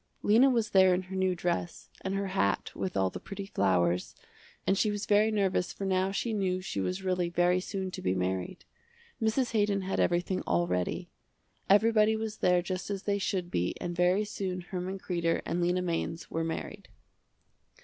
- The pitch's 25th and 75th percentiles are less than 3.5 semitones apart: Yes, narrow, 2.6 semitones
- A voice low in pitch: No, medium, 185 Hz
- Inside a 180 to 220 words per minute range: Yes, average, 190 wpm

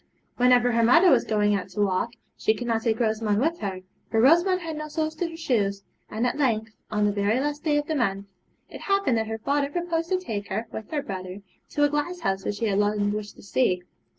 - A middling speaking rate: No, fast, 235 wpm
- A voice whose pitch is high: Yes, high, 230 Hz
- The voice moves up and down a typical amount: No, wide, 6.2 semitones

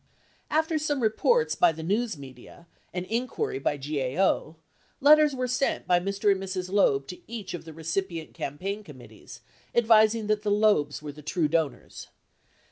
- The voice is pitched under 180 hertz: No, high, 190 Hz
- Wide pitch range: Yes, wide, 6.2 semitones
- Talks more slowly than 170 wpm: Yes, average, 160 wpm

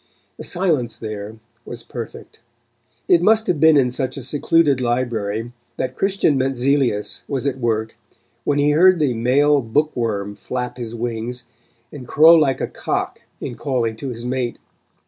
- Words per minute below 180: Yes, average, 160 wpm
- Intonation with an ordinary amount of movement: Yes, average, 3.8 semitones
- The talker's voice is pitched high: No, low, 130 Hz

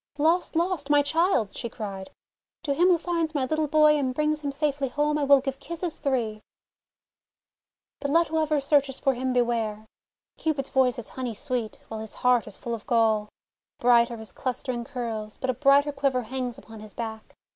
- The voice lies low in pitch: No, very high, 265 Hz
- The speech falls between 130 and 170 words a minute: No, average, 190 wpm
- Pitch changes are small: No, average, 4.2 semitones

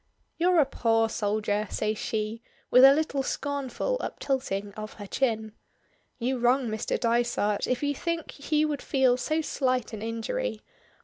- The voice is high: Yes, very high, 250 Hz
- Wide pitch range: No, average, 4.6 semitones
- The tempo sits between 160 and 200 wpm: No, average, 150 wpm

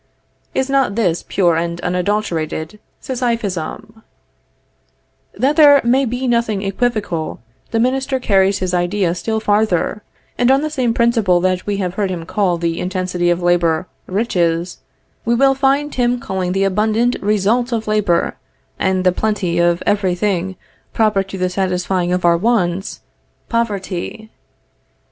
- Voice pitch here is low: No, high, 200 Hz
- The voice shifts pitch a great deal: No, average, 4.6 semitones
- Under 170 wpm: Yes, average, 145 wpm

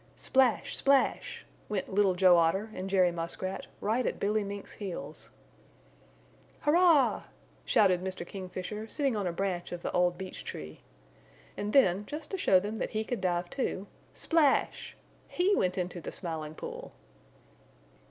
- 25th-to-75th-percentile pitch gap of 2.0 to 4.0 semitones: Yes, average, 3.7 semitones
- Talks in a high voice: Yes, high, 195 Hz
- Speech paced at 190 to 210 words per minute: No, average, 150 wpm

